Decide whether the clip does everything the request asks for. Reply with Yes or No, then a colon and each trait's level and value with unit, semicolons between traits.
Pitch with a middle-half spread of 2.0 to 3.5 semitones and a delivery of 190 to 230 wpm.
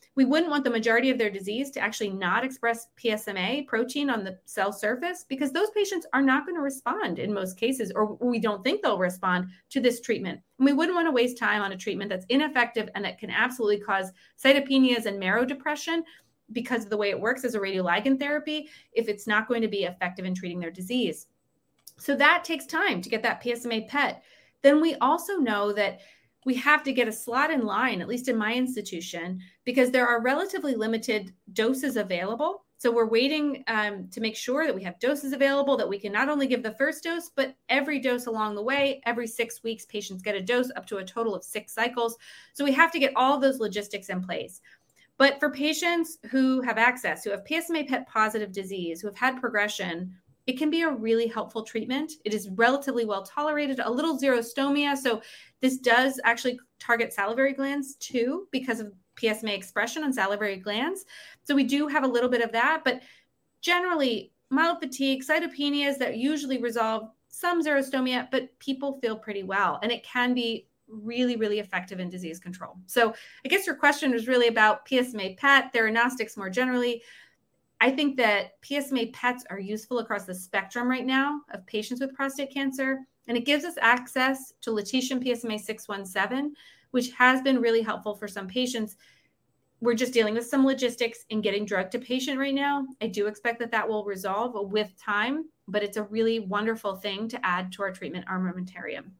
No: average, 4.4 semitones; average, 195 wpm